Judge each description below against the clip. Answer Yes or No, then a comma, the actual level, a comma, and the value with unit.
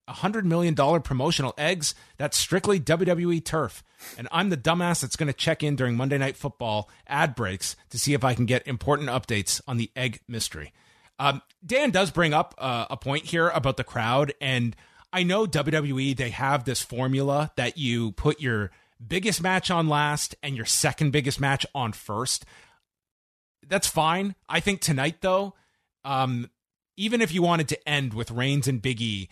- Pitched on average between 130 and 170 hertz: Yes, medium, 140 Hz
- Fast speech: No, average, 175 wpm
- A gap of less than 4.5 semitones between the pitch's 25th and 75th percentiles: No, average, 4.8 semitones